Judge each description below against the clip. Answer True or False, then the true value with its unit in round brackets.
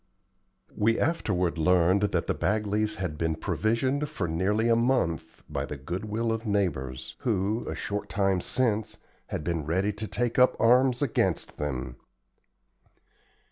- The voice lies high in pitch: False (105 Hz)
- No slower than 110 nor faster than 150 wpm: True (145 wpm)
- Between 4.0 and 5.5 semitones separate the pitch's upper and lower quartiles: True (5.1 semitones)